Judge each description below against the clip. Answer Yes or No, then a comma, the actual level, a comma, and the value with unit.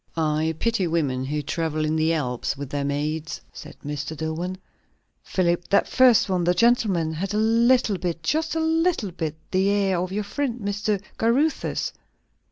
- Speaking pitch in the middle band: Yes, medium, 180 Hz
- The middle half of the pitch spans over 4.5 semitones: Yes, wide, 5.6 semitones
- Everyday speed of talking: Yes, average, 170 wpm